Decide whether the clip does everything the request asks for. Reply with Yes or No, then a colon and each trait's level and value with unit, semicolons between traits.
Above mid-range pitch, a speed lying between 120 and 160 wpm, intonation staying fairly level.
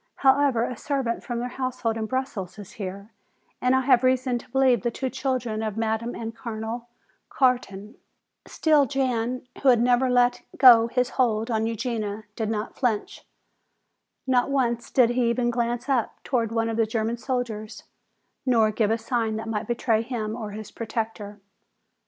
No: high, 235 Hz; average, 170 wpm; narrow, 2.3 semitones